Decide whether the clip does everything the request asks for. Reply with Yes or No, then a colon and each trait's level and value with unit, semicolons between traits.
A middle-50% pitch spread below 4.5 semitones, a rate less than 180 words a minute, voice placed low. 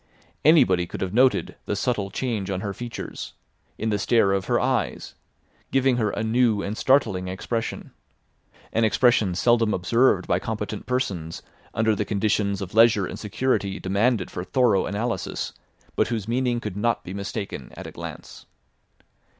Yes: average, 3.5 semitones; average, 160 wpm; low, 105 Hz